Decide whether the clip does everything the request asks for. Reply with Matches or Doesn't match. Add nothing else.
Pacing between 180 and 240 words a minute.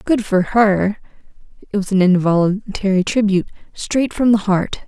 Doesn't match